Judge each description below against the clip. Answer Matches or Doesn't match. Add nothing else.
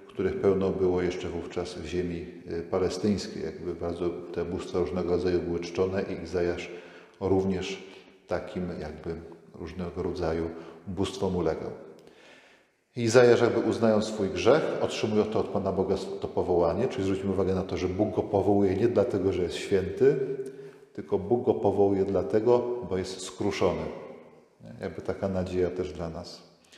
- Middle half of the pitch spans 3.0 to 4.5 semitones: Doesn't match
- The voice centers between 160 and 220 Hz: Doesn't match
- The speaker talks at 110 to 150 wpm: Matches